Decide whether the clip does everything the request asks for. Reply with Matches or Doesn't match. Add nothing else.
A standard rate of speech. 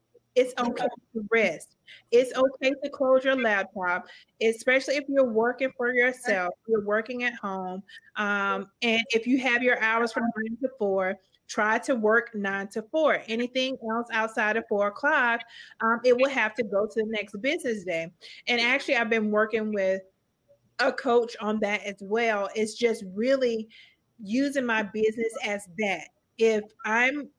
Matches